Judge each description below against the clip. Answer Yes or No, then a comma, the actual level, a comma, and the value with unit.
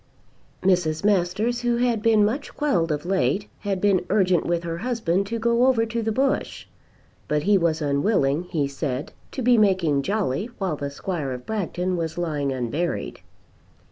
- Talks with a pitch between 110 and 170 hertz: No, medium, 185 Hz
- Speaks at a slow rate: No, average, 170 wpm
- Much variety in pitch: Yes, wide, 5.8 semitones